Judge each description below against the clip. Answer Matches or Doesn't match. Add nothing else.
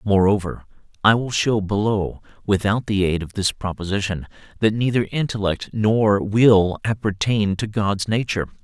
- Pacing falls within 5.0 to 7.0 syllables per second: Doesn't match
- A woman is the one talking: Doesn't match